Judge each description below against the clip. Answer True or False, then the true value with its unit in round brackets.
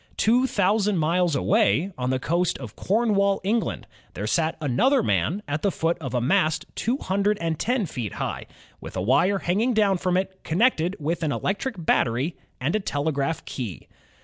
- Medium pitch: True (180 Hz)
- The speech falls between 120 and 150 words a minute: False (180 wpm)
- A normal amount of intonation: False (5.7 semitones)